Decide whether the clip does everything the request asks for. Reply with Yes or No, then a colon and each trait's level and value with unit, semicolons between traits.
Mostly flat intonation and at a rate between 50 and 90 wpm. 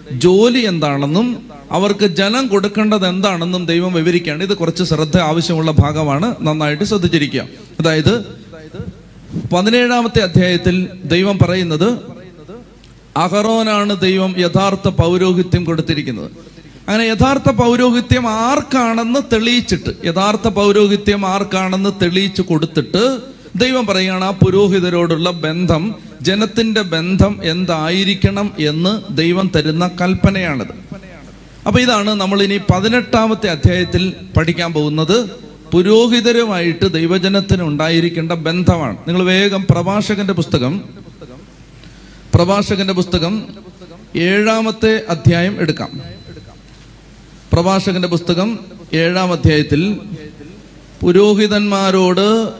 No: average, 3.7 semitones; average, 85 wpm